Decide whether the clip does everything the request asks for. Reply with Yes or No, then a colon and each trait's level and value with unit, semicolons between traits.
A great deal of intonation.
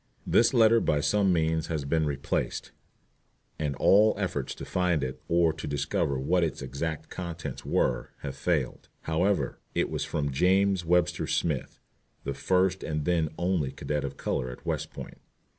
No: average, 4.1 semitones